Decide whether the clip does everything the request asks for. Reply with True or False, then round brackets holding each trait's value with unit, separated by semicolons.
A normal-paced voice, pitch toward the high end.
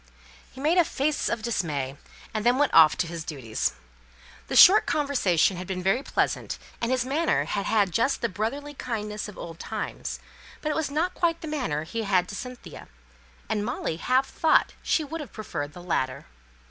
True (190 wpm; 225 Hz)